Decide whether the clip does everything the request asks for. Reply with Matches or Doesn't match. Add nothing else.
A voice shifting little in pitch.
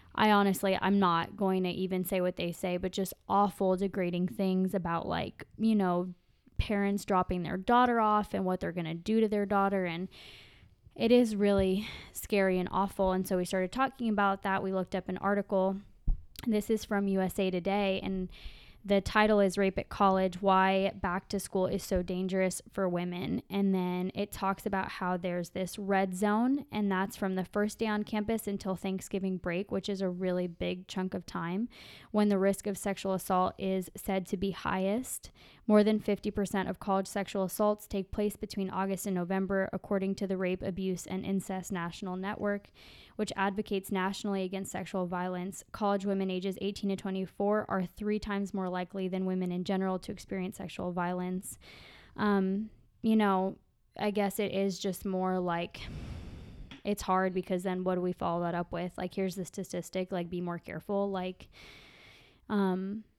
Matches